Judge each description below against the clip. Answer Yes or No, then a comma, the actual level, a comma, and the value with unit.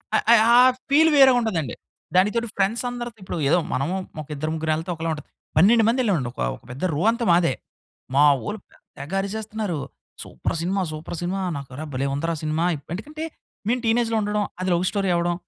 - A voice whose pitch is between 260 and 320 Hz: No, high, 190 Hz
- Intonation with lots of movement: Yes, wide, 5.8 semitones